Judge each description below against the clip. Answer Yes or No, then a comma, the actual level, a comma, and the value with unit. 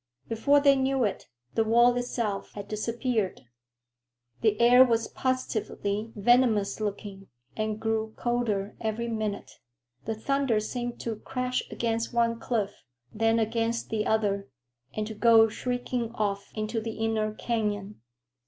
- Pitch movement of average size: No, narrow, 2.1 semitones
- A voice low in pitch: No, high, 225 Hz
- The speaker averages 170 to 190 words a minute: No, slow, 135 wpm